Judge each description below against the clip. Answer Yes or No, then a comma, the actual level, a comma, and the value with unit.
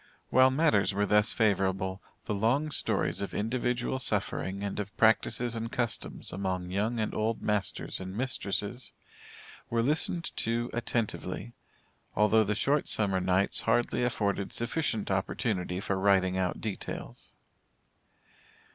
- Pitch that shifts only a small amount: No, average, 3.4 semitones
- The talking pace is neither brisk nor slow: No, slow, 130 wpm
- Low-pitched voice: Yes, low, 105 Hz